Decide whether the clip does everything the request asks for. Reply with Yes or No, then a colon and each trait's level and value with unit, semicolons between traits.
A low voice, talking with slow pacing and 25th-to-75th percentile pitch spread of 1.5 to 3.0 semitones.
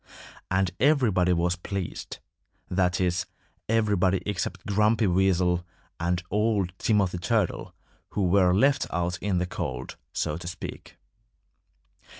Yes: very low, 95 Hz; slow, 120 wpm; narrow, 2.6 semitones